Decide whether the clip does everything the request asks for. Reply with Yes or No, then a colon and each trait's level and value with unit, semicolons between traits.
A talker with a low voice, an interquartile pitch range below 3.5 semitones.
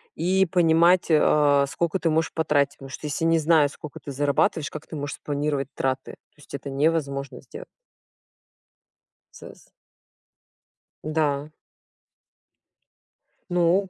No: medium, 150 Hz; average, 2.7 semitones